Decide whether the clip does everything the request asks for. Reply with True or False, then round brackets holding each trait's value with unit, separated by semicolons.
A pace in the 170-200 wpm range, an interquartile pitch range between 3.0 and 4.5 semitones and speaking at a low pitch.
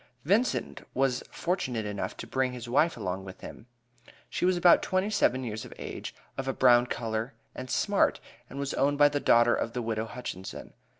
True (190 wpm; 4.0 semitones; 125 Hz)